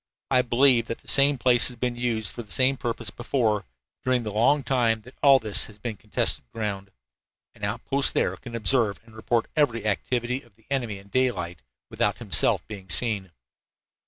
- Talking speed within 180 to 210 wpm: Yes, average, 185 wpm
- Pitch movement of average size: Yes, average, 3.2 semitones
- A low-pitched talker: Yes, low, 115 Hz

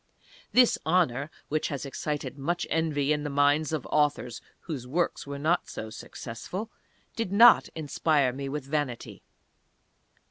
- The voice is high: No, medium, 150 Hz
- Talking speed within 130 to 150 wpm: Yes, average, 140 wpm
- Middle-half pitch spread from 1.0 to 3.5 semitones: Yes, average, 2.7 semitones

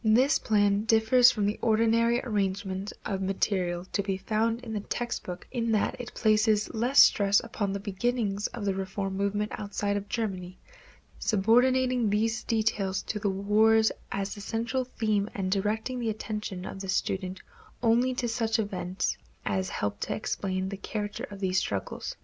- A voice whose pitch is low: No, high, 210 Hz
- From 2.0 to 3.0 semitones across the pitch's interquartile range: Yes, narrow, 2.6 semitones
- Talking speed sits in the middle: Yes, average, 165 wpm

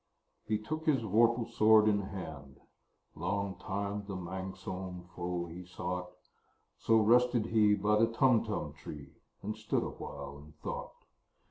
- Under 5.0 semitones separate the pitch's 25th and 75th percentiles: Yes, average, 3.4 semitones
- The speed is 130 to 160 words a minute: Yes, slow, 135 wpm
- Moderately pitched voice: No, low, 100 Hz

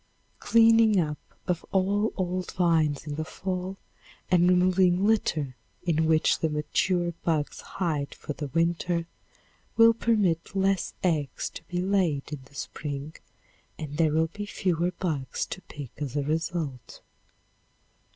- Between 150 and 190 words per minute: No, average, 140 wpm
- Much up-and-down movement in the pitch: No, average, 3.7 semitones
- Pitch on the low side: No, medium, 170 Hz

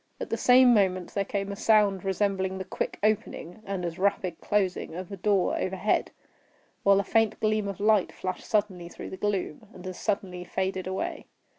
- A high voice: Yes, high, 195 Hz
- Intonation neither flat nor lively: No, narrow, 2.0 semitones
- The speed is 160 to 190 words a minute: Yes, average, 185 wpm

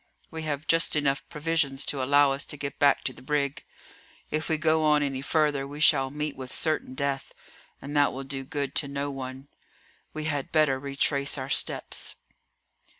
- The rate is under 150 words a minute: No, average, 185 wpm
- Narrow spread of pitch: Yes, narrow, 1.8 semitones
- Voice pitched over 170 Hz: No, medium, 140 Hz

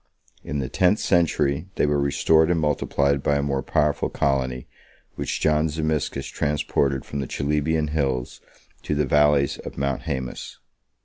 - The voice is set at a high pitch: No, very low, 70 Hz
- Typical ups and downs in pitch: No, narrow, 1.7 semitones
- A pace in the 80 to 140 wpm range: No, average, 165 wpm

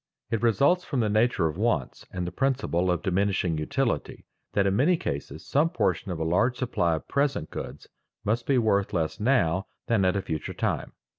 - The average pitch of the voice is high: No, low, 100 Hz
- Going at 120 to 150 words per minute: No, average, 195 wpm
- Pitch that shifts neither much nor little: No, wide, 6.2 semitones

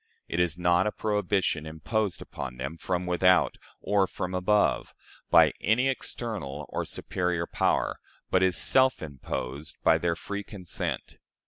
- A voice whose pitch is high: No, very low, 90 Hz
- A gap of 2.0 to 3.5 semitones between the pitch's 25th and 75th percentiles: No, average, 4.3 semitones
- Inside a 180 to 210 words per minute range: No, average, 140 wpm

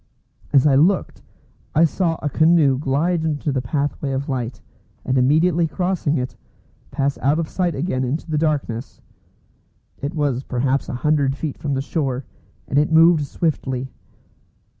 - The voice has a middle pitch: Yes, medium, 145 Hz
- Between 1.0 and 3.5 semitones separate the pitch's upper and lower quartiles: Yes, average, 3.2 semitones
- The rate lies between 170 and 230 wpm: No, average, 155 wpm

